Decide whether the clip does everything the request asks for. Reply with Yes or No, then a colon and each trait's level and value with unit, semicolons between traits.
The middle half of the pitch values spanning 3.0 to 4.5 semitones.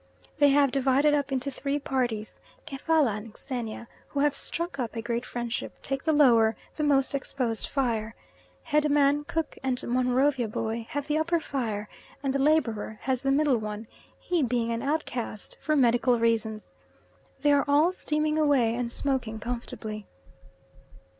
Yes: average, 4.0 semitones